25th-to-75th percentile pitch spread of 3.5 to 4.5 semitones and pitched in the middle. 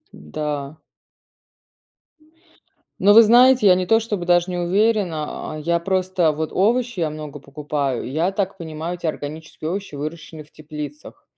Yes: average, 4.2 semitones; medium, 170 Hz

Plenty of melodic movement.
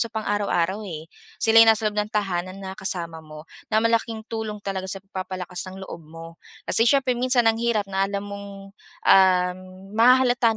No: average, 3.3 semitones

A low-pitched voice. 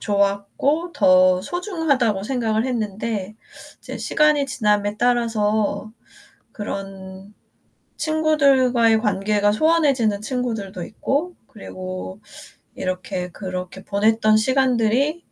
No: high, 215 Hz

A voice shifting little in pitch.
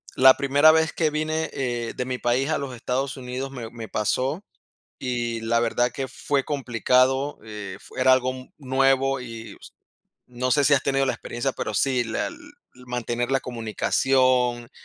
Yes: narrow, 2.1 semitones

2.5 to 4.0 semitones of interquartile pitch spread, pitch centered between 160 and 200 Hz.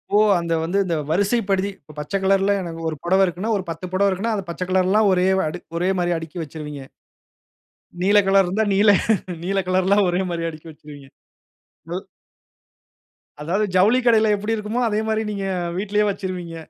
Yes: average, 2.9 semitones; high, 190 Hz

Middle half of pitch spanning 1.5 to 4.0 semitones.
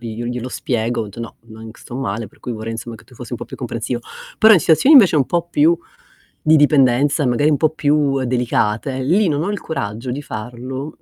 No: average, 4.7 semitones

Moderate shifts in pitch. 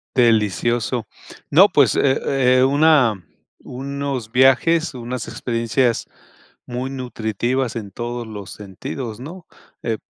Yes: average, 3.1 semitones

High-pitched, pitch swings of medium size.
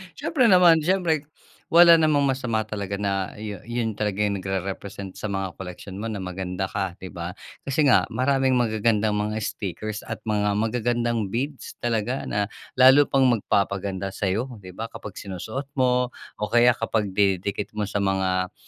No: low, 105 Hz; average, 4.3 semitones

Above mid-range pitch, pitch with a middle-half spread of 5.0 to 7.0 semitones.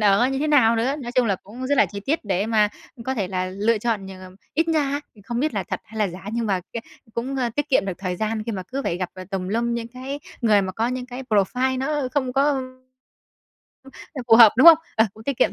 No: high, 235 Hz; average, 4.5 semitones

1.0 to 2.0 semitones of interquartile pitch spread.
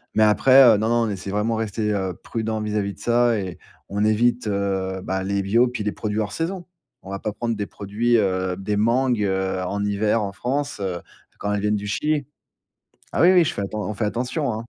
No: average, 2.9 semitones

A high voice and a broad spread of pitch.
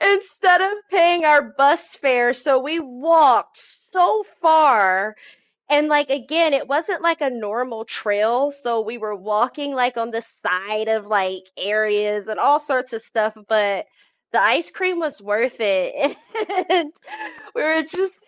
Yes: very high, 260 Hz; wide, 6.5 semitones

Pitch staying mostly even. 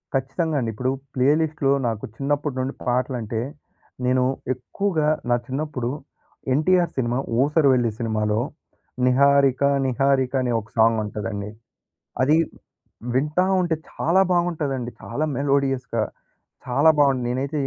No: average, 3.3 semitones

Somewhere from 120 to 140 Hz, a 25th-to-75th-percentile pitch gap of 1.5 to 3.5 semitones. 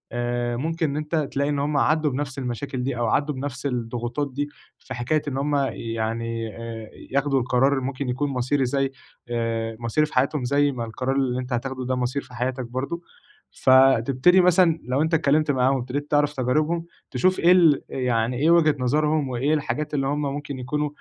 Yes: low, 135 Hz; average, 3.1 semitones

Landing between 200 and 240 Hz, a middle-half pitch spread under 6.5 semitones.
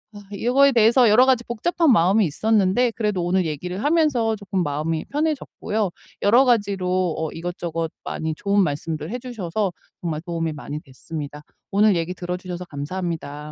No: medium, 185 Hz; wide, 5.4 semitones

